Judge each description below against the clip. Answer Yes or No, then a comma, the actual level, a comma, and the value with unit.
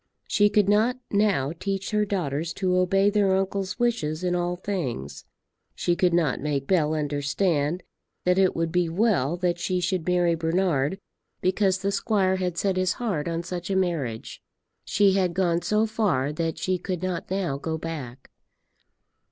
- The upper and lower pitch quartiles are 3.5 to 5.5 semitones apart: No, average, 3.1 semitones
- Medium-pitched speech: Yes, medium, 180 Hz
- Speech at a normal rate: Yes, average, 170 wpm